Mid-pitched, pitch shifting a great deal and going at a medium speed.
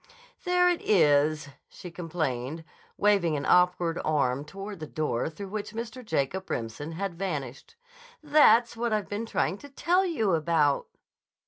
Yes: medium, 180 Hz; wide, 6.1 semitones; average, 145 wpm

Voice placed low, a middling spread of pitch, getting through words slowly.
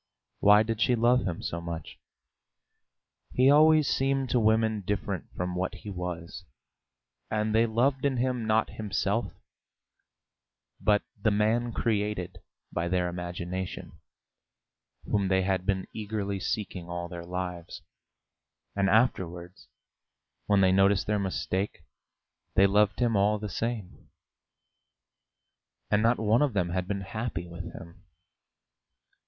Yes: low, 100 Hz; average, 3.5 semitones; slow, 130 wpm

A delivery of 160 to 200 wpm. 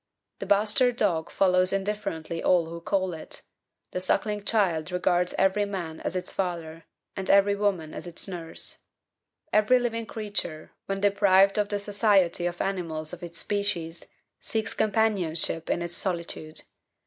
No: average, 150 wpm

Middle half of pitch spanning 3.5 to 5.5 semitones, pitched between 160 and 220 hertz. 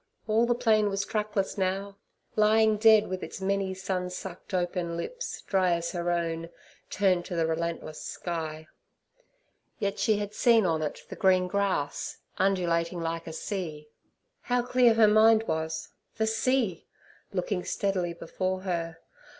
Yes: average, 3.9 semitones; high, 190 Hz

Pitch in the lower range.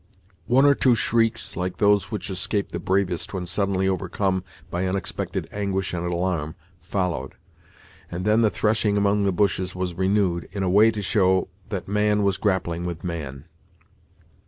Yes: very low, 95 Hz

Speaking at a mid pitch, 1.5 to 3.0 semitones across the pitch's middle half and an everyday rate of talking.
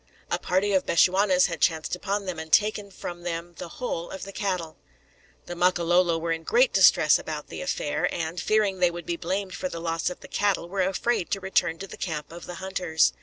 No: medium, 180 Hz; narrow, 2.6 semitones; fast, 220 wpm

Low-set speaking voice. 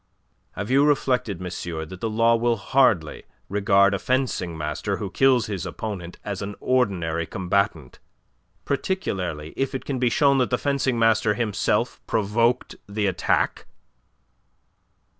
Yes: low, 105 Hz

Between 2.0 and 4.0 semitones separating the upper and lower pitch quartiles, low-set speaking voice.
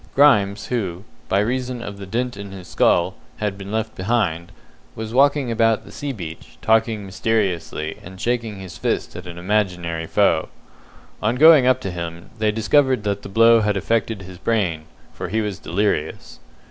Yes: average, 3.7 semitones; low, 105 Hz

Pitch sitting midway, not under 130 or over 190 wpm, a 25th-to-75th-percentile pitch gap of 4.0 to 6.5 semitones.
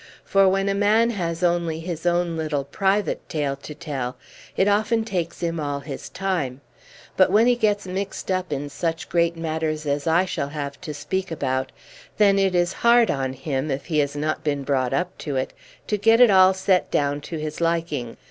No: medium, 170 Hz; average, 200 wpm; average, 4.8 semitones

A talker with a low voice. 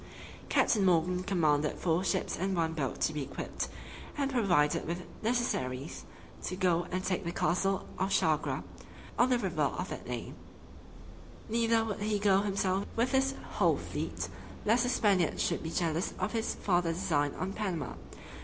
No: medium, 185 Hz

